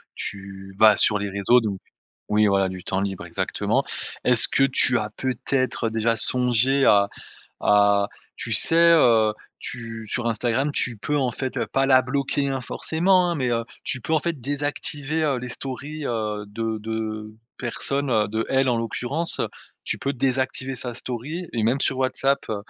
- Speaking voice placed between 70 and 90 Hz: No, low, 120 Hz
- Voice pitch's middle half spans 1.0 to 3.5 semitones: No, average, 4.0 semitones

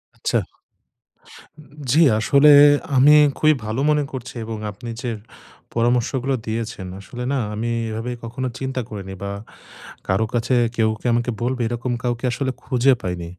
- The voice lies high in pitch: No, low, 120 Hz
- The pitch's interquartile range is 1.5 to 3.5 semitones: Yes, average, 2.9 semitones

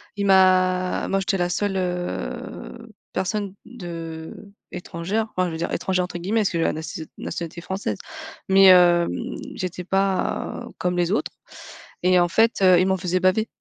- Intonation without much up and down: Yes, narrow, 1.7 semitones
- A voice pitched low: No, medium, 185 Hz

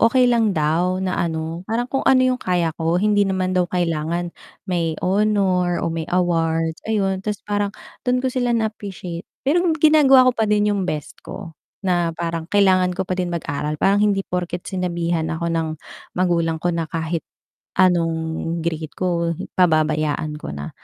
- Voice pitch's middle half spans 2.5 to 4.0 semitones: Yes, average, 3.6 semitones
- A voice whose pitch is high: No, medium, 180 Hz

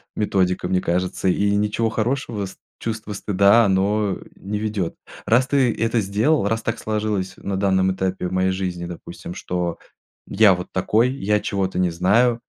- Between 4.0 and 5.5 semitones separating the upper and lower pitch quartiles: No, average, 2.9 semitones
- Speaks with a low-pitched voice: Yes, low, 100 Hz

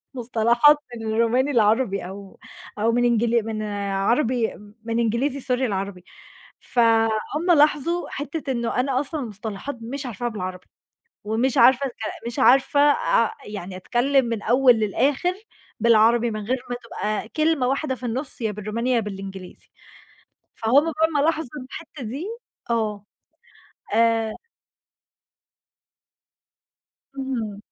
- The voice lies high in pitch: Yes, high, 235 Hz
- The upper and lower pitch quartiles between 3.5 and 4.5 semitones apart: Yes, average, 3.8 semitones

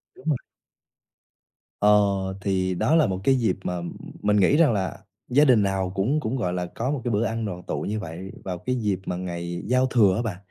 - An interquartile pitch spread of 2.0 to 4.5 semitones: No, average, 4.9 semitones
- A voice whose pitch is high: No, low, 105 Hz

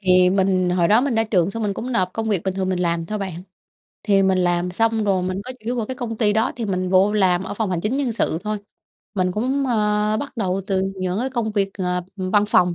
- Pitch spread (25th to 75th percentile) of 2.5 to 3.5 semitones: Yes, average, 3.2 semitones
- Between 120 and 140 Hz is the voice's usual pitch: No, high, 195 Hz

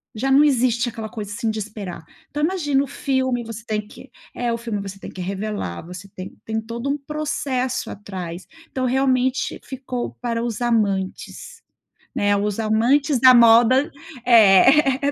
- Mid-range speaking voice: No, high, 235 Hz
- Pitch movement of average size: Yes, average, 4.0 semitones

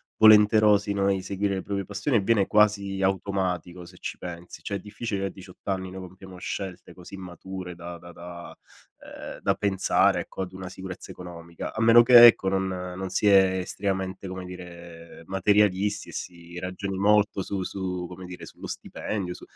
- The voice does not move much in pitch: Yes, narrow, 1.8 semitones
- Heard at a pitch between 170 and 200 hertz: No, very low, 95 Hz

